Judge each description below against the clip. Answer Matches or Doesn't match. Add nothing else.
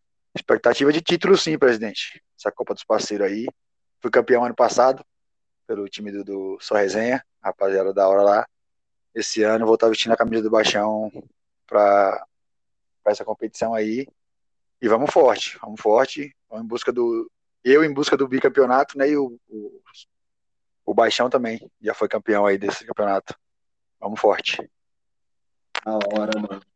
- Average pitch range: Matches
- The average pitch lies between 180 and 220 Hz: Doesn't match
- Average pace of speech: Matches